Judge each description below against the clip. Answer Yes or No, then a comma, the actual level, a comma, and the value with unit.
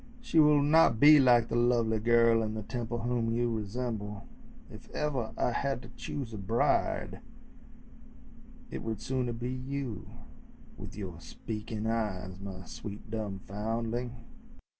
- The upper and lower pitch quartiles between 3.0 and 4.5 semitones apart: No, narrow, 2.4 semitones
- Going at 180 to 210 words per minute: No, average, 140 wpm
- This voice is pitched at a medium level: No, low, 115 Hz